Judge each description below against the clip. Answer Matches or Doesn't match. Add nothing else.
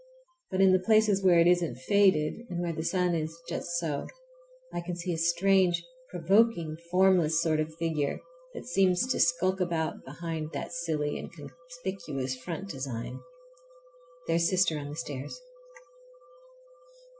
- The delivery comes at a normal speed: Matches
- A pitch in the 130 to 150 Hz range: Doesn't match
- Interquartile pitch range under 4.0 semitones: Matches